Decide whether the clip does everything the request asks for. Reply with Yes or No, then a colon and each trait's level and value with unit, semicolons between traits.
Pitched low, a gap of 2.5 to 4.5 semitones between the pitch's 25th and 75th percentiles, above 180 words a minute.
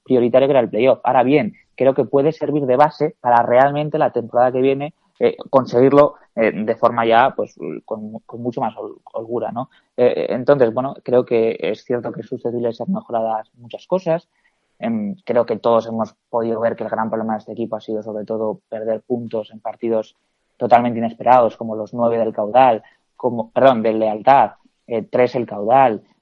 Yes: low, 120 Hz; average, 3.9 semitones; fast, 190 wpm